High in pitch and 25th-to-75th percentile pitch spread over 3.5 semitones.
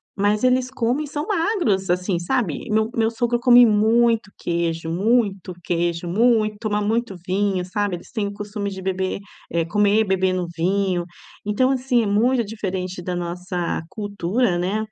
Yes: high, 205 Hz; average, 4.1 semitones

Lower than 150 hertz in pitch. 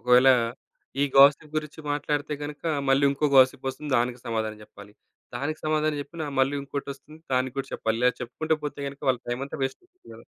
Yes: medium, 140 Hz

